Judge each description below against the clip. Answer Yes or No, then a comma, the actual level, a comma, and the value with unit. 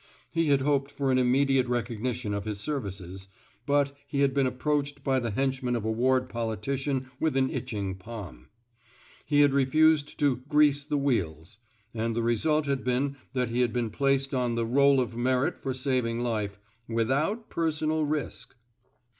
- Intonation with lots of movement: No, average, 3.4 semitones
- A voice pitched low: Yes, low, 130 Hz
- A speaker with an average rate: Yes, average, 170 wpm